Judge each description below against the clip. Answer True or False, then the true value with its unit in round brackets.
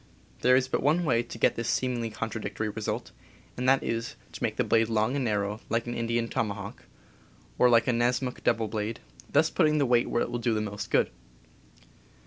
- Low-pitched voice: True (115 Hz)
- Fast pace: True (210 wpm)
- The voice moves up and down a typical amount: False (2.2 semitones)